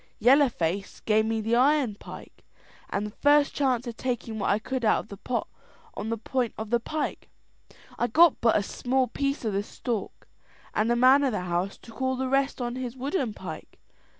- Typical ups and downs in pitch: Yes, average, 3.6 semitones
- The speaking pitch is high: Yes, high, 240 Hz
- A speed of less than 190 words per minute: No, fast, 205 wpm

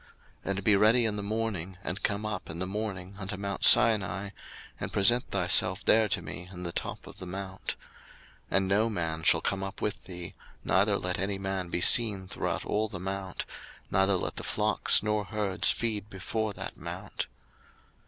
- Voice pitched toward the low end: Yes, very low, 95 Hz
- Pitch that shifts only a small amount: Yes, narrow, 2.3 semitones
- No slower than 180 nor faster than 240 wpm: Yes, average, 190 wpm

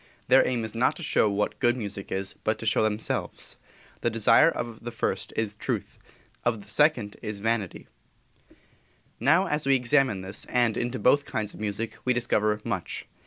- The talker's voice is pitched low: Yes, low, 115 Hz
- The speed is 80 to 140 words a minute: No, average, 185 wpm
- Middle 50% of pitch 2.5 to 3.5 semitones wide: Yes, average, 2.8 semitones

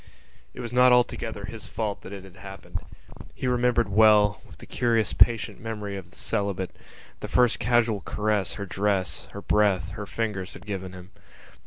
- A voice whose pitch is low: Yes, low, 105 Hz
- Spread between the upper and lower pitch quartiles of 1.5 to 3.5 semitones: Yes, narrow, 2.6 semitones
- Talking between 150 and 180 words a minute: Yes, average, 175 wpm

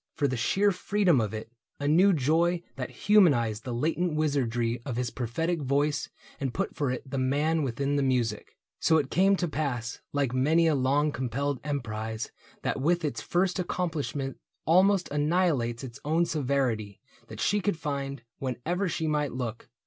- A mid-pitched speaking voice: Yes, medium, 145 Hz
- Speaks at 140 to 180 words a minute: Yes, average, 170 wpm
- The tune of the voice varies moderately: Yes, average, 4.7 semitones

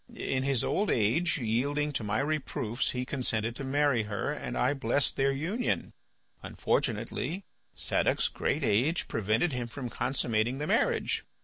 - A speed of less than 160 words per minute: Yes, average, 145 wpm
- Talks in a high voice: No, low, 130 Hz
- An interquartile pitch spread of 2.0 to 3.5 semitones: No, average, 4.2 semitones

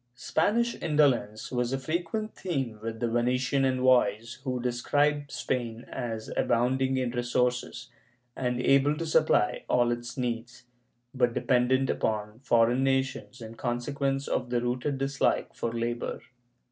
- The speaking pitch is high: No, low, 125 Hz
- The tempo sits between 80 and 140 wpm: Yes, slow, 135 wpm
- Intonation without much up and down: Yes, narrow, 2.2 semitones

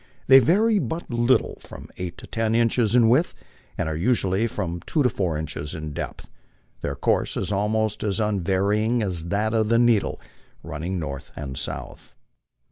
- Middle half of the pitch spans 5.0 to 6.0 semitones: Yes, average, 5.3 semitones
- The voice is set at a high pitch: No, low, 105 Hz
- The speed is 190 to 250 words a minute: No, average, 170 wpm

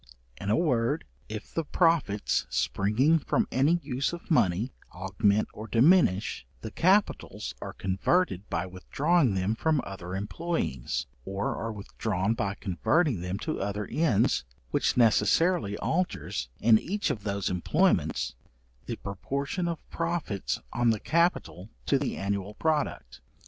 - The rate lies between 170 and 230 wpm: No, slow, 135 wpm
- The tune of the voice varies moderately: No, wide, 8.3 semitones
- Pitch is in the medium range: No, low, 110 Hz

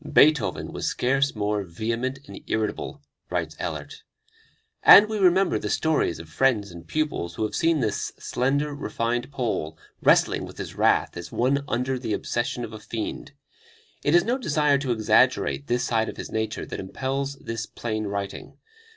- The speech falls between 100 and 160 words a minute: No, average, 170 wpm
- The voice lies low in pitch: Yes, low, 120 Hz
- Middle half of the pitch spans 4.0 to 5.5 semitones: Yes, average, 5.2 semitones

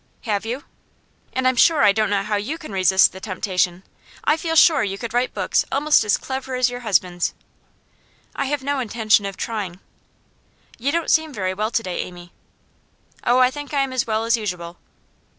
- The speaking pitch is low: No, high, 225 Hz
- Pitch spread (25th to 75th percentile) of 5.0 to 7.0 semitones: Yes, average, 5.3 semitones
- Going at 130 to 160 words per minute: No, average, 195 wpm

